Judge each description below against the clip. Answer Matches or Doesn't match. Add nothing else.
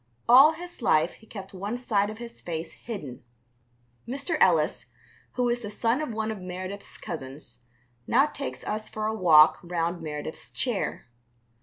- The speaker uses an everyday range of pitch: Doesn't match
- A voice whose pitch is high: Matches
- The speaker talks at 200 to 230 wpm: Doesn't match